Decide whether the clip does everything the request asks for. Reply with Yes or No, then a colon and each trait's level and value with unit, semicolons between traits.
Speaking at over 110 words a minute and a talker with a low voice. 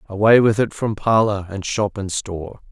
Yes: average, 200 wpm; low, 105 Hz